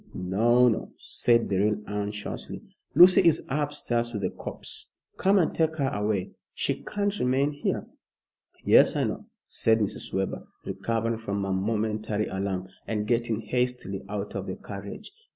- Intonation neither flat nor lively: Yes, average, 3.9 semitones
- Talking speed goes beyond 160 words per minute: No, average, 150 wpm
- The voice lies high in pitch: No, low, 110 Hz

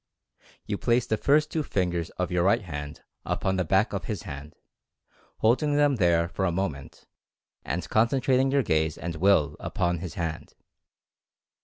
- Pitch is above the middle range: No, very low, 95 Hz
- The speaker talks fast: No, average, 165 wpm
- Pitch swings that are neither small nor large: No, wide, 5.7 semitones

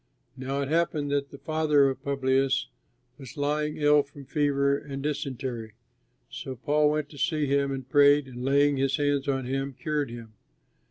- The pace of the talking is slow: No, average, 170 wpm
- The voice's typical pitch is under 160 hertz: Yes, medium, 140 Hz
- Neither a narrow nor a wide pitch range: No, narrow, 1.6 semitones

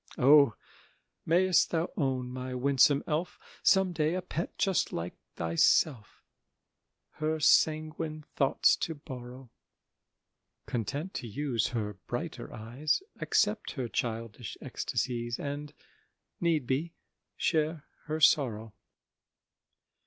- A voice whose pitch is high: No, medium, 145 Hz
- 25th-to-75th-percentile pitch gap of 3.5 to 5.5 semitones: Yes, average, 4.6 semitones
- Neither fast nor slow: No, slow, 105 wpm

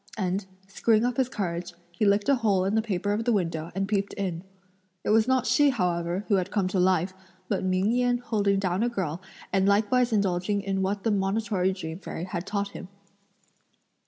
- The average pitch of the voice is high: Yes, high, 200 Hz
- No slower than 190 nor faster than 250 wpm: Yes, average, 200 wpm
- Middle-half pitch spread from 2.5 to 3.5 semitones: Yes, average, 2.8 semitones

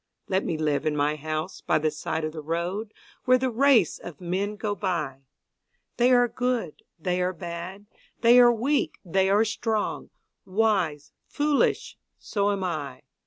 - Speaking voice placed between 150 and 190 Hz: Yes, medium, 185 Hz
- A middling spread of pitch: No, wide, 6.0 semitones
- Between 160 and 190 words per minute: Yes, average, 165 wpm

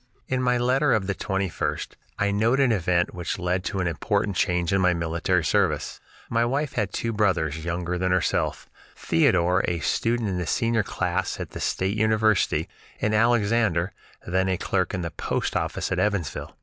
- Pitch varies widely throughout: No, average, 3.7 semitones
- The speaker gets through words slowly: No, average, 180 wpm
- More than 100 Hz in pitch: No, very low, 95 Hz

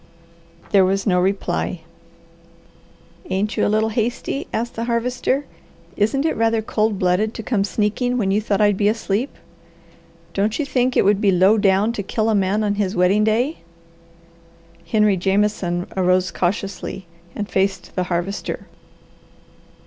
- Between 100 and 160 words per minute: Yes, average, 150 wpm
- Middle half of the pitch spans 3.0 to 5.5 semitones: No, narrow, 2.6 semitones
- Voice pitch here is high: Yes, high, 205 Hz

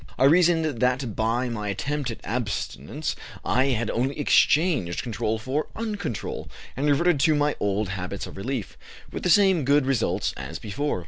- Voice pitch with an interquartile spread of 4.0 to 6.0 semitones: Yes, average, 5.2 semitones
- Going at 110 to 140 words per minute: No, average, 165 wpm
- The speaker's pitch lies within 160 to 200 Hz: No, low, 130 Hz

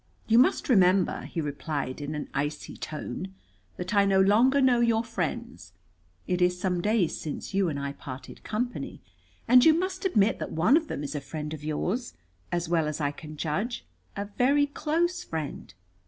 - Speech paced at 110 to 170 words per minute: No, average, 185 wpm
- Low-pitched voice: No, high, 190 Hz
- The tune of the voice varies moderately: No, wide, 7.7 semitones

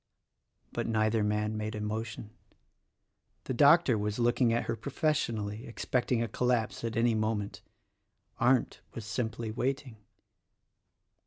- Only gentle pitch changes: Yes, narrow, 2.2 semitones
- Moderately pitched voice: No, low, 115 Hz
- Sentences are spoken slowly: Yes, slow, 125 wpm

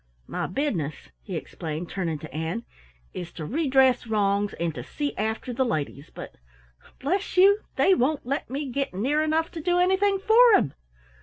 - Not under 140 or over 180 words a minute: Yes, average, 170 wpm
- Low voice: No, very high, 260 Hz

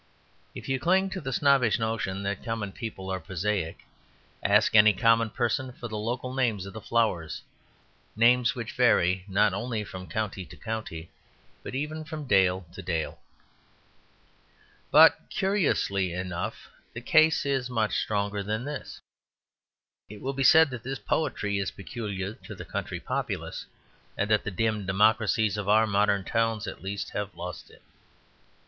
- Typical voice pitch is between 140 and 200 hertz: No, low, 110 Hz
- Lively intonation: No, average, 4.1 semitones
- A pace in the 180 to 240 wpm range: No, average, 155 wpm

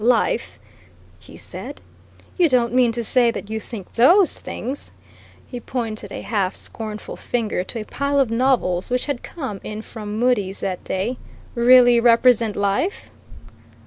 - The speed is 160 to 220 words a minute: No, average, 150 wpm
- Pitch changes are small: No, average, 3.0 semitones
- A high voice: Yes, high, 235 Hz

